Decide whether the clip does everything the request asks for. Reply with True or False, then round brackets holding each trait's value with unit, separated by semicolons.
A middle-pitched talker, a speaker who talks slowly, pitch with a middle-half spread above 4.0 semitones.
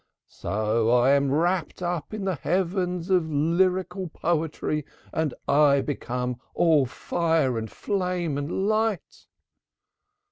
True (160 Hz; 115 wpm; 4.5 semitones)